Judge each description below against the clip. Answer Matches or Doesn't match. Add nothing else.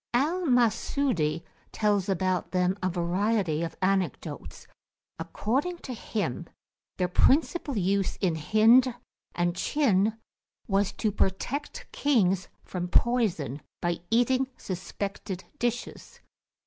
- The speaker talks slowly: Matches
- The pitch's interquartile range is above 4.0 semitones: Matches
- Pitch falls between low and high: Doesn't match